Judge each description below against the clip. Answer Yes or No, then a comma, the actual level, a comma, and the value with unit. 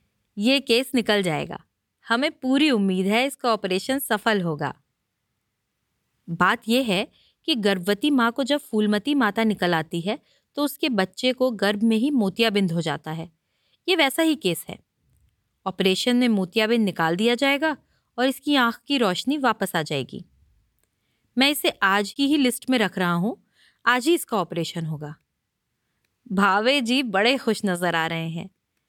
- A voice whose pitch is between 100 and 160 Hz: No, high, 220 Hz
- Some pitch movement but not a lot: No, wide, 6.2 semitones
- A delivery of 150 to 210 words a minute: Yes, average, 160 wpm